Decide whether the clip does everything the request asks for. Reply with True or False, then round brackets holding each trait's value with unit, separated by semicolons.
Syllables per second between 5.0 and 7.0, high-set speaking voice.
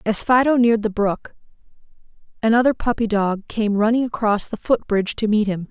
True (5.5 syllables/s; 220 Hz)